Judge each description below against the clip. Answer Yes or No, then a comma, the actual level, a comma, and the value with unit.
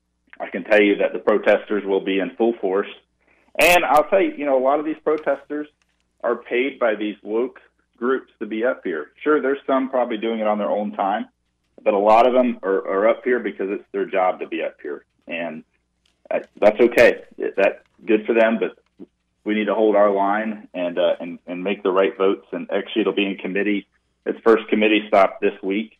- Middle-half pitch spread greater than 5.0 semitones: Yes, wide, 5.6 semitones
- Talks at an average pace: No, fast, 215 wpm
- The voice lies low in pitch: Yes, low, 105 Hz